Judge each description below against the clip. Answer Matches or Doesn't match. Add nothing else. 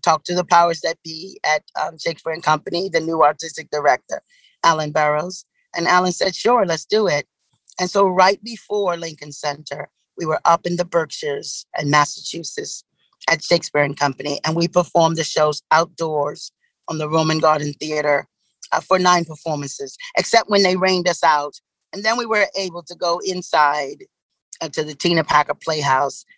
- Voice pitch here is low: Doesn't match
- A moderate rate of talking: Matches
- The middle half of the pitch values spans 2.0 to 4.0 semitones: Matches